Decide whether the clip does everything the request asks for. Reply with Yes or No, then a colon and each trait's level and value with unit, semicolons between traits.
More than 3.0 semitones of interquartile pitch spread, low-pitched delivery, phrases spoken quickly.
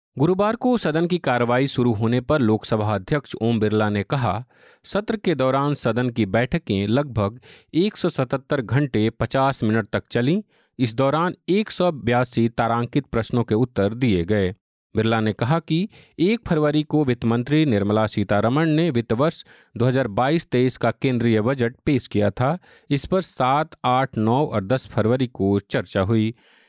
No: average, 5.1 semitones; low, 125 Hz; average, 155 wpm